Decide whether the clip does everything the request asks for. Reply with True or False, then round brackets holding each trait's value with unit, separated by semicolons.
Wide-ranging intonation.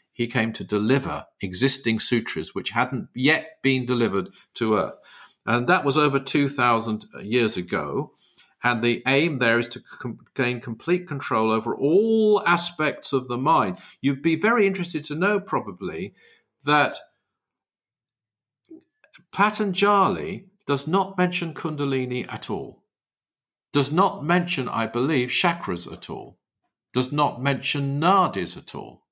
True (6.4 semitones)